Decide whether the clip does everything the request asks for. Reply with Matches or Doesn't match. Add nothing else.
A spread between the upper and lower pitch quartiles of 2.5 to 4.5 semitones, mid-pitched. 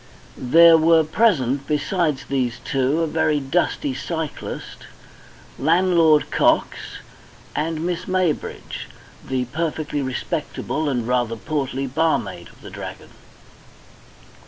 Matches